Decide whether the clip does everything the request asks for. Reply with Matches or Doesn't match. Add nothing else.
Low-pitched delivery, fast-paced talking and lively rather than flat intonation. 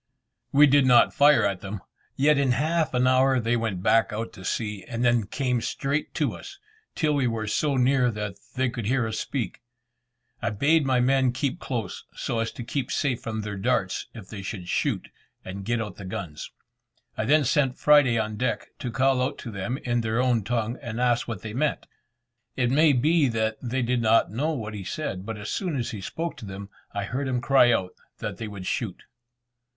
Doesn't match